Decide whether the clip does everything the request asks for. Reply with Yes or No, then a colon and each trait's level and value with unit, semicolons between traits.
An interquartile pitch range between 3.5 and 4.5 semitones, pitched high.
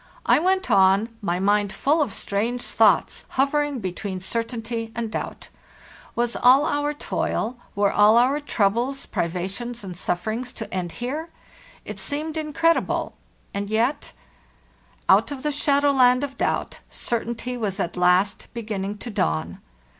No: wide, 5.6 semitones; high, 235 Hz